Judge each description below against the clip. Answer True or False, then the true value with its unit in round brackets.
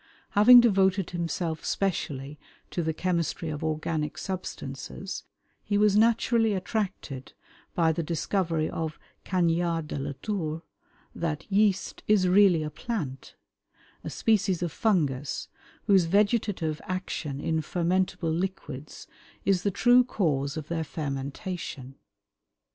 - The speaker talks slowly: True (120 wpm)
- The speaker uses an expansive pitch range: False (4.2 semitones)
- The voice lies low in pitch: False (170 Hz)